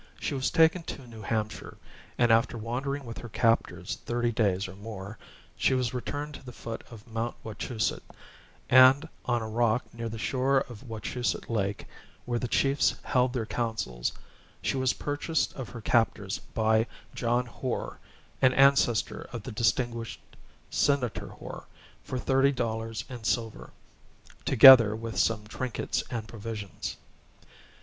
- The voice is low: Yes, low, 120 Hz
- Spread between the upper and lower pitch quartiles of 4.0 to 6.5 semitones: No, narrow, 2.5 semitones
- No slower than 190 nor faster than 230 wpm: No, average, 145 wpm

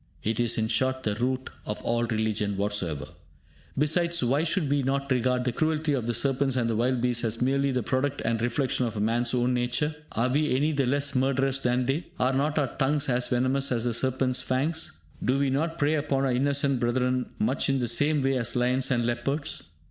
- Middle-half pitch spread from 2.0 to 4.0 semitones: Yes, average, 2.7 semitones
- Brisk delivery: Yes, fast, 210 wpm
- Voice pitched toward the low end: Yes, low, 130 Hz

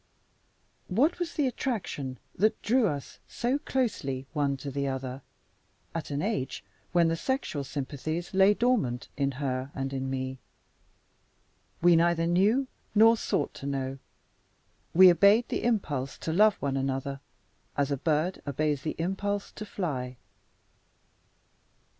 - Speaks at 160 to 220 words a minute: No, slow, 135 wpm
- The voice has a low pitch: No, medium, 155 Hz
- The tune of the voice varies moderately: No, wide, 6.9 semitones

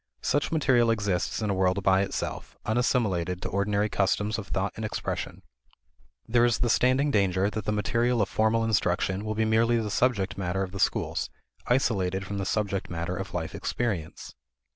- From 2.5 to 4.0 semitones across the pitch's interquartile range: Yes, average, 3.2 semitones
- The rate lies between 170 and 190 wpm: Yes, average, 180 wpm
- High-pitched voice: No, low, 105 Hz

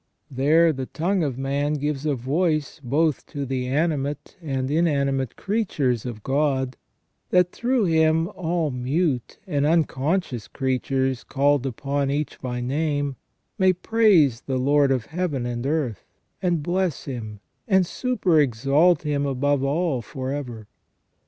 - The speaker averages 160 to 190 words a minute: No, slow, 135 wpm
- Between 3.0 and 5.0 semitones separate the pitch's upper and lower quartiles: Yes, average, 3.7 semitones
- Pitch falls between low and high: Yes, medium, 145 Hz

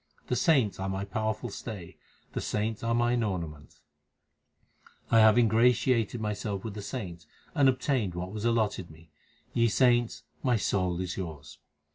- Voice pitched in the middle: No, low, 105 Hz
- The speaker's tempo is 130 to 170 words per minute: Yes, average, 150 wpm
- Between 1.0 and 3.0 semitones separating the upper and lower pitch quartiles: No, average, 4.3 semitones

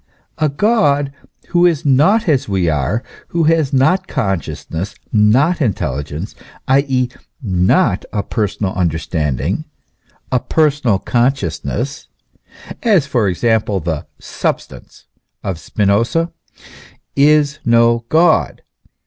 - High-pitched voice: No, low, 125 Hz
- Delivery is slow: Yes, slow, 100 wpm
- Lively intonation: Yes, wide, 7.7 semitones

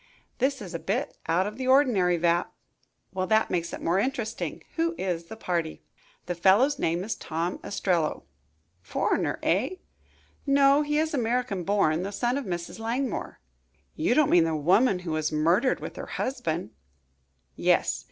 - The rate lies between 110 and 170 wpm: Yes, average, 160 wpm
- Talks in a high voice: Yes, high, 195 Hz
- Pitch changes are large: Yes, wide, 7.0 semitones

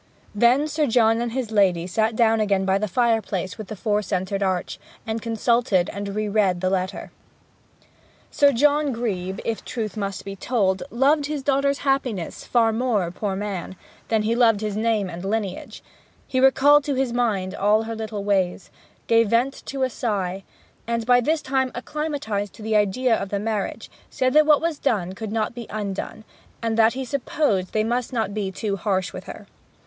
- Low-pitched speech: No, high, 220 Hz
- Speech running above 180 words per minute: Yes, average, 190 wpm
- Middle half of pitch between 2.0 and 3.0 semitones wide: No, average, 3.9 semitones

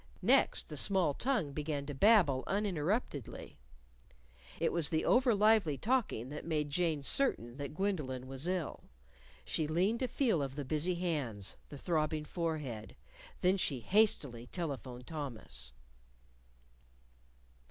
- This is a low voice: No, medium, 155 Hz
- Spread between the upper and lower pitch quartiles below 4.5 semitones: No, wide, 5.4 semitones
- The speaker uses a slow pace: Yes, slow, 125 wpm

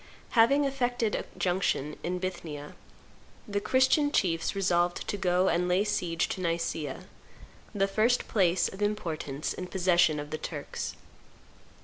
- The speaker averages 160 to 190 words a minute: No, slow, 135 wpm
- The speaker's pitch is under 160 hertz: No, medium, 180 Hz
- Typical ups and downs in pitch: Yes, average, 3.8 semitones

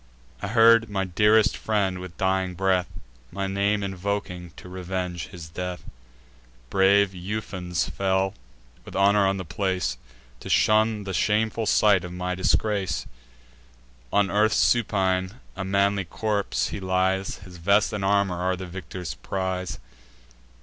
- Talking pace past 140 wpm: No, slow, 135 wpm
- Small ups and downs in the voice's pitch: Yes, narrow, 1.8 semitones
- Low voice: Yes, very low, 95 Hz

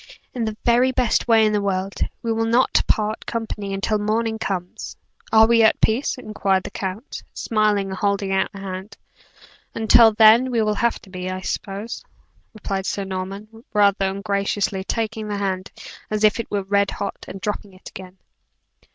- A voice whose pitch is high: Yes, high, 210 Hz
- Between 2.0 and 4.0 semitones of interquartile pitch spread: Yes, narrow, 2.4 semitones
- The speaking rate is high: No, average, 175 wpm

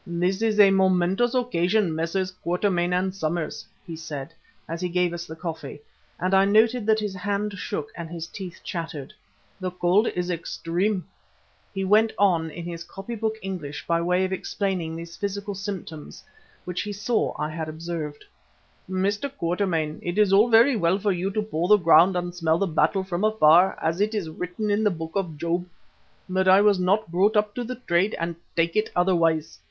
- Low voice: No, medium, 180 Hz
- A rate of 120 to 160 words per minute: No, average, 185 wpm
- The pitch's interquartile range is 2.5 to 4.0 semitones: Yes, average, 3.3 semitones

